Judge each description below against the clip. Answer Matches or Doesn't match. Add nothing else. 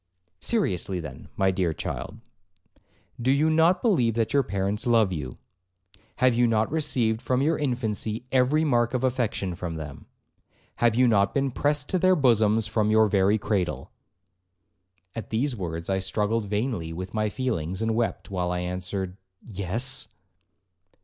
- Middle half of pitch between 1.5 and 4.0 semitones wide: Doesn't match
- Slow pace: Doesn't match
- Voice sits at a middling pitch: Doesn't match